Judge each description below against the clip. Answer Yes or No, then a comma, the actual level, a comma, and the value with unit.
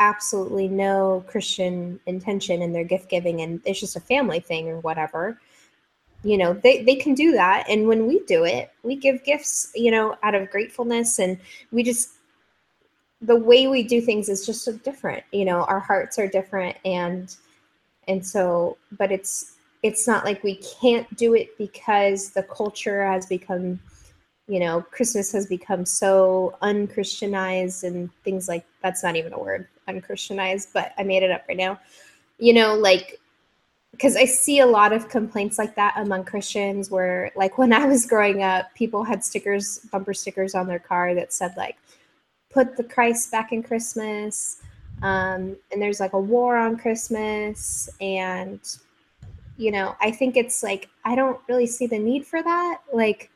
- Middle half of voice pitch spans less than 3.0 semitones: No, average, 3.8 semitones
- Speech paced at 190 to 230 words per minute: No, average, 175 wpm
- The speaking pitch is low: No, high, 205 Hz